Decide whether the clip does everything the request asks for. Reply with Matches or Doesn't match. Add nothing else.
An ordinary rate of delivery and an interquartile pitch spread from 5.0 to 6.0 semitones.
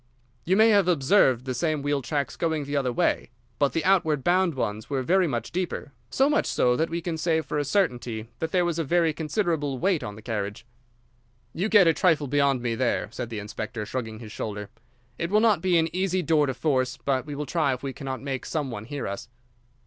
Doesn't match